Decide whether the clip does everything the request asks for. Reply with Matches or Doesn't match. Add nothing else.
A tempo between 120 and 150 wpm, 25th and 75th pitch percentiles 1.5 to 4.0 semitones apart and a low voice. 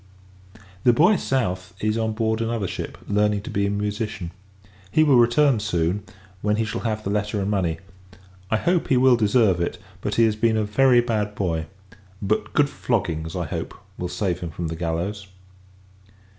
Doesn't match